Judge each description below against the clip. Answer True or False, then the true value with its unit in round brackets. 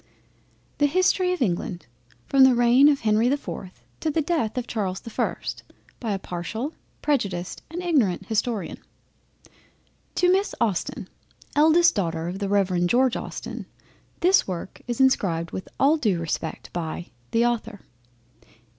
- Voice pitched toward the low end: False (230 Hz)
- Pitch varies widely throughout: True (7.4 semitones)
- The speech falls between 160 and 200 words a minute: False (145 wpm)